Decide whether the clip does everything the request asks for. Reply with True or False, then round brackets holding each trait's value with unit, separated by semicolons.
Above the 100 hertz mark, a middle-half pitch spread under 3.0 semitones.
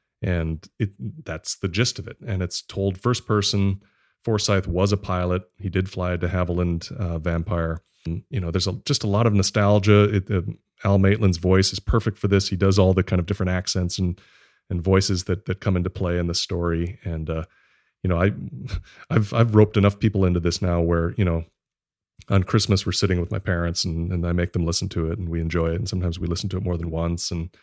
False (95 Hz; 2.6 semitones)